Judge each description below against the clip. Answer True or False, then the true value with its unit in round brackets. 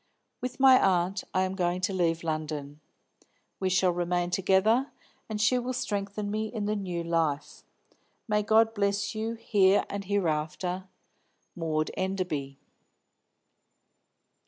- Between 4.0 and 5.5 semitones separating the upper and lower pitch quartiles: False (3.6 semitones)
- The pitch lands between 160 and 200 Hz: True (190 Hz)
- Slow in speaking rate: True (130 wpm)